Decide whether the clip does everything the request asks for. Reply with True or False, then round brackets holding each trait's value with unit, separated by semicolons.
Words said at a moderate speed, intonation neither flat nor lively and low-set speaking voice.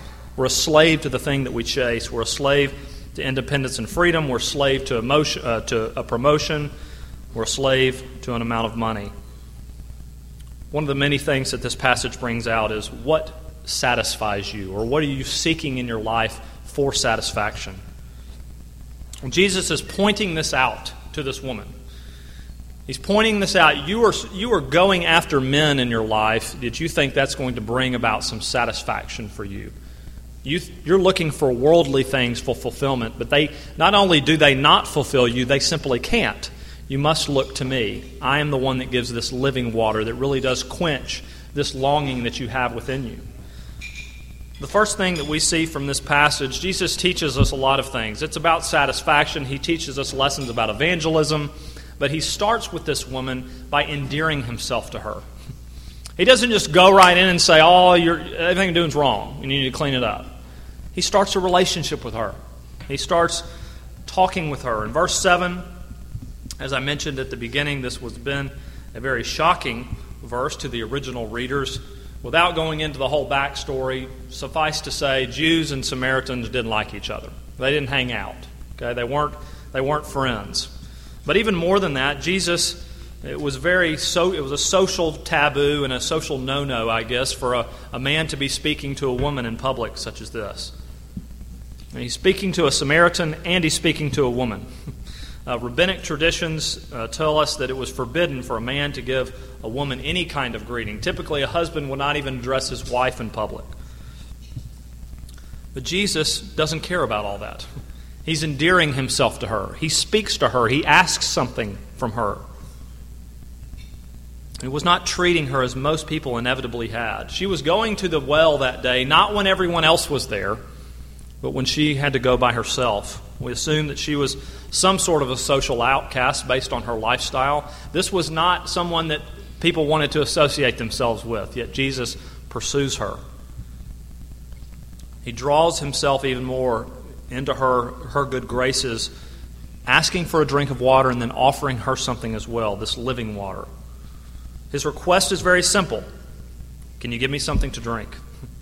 False (180 wpm; 5.9 semitones; 130 Hz)